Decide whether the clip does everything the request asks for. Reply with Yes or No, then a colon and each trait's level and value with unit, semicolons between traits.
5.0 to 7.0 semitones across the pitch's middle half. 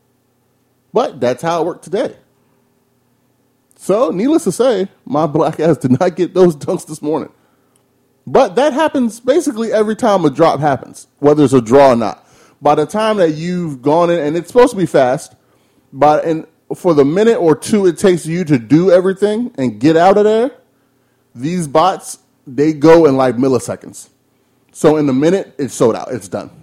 Yes: wide, 5.6 semitones